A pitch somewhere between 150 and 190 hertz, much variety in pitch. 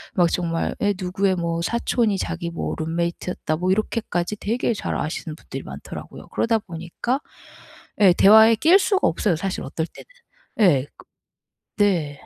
No: medium, 185 Hz; average, 4.4 semitones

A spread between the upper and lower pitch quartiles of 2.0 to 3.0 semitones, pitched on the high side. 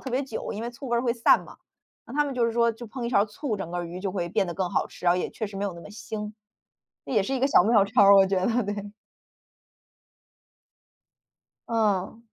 No: average, 3.4 semitones; high, 215 Hz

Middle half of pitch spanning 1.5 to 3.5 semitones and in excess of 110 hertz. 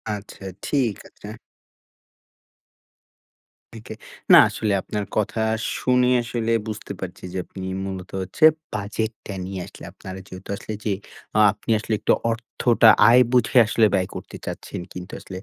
No: average, 3.1 semitones; low, 105 Hz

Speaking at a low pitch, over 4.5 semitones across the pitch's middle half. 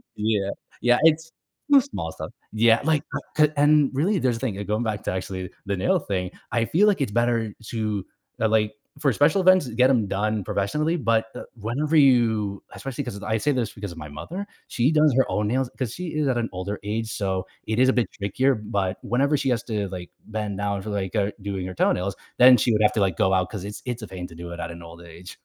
Yes: low, 110 Hz; average, 5.0 semitones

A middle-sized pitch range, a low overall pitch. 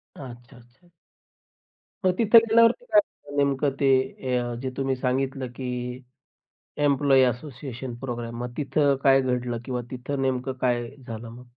No: narrow, 2.3 semitones; low, 130 Hz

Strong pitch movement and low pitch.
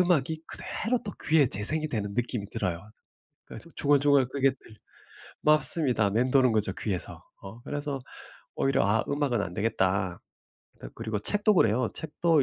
Yes: wide, 6.0 semitones; low, 125 Hz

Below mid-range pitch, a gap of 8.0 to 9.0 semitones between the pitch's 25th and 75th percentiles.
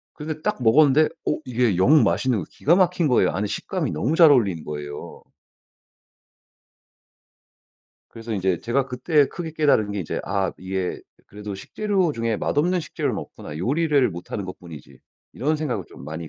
Yes: low, 120 Hz; wide, 8.3 semitones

